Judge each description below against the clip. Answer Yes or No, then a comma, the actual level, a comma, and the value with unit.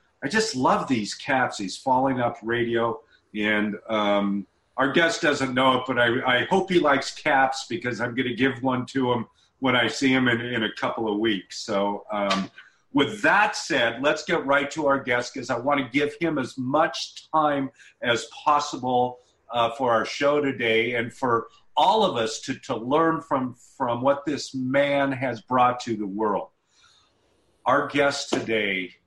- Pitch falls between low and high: No, low, 125 Hz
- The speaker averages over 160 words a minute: Yes, average, 185 wpm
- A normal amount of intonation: Yes, average, 3.4 semitones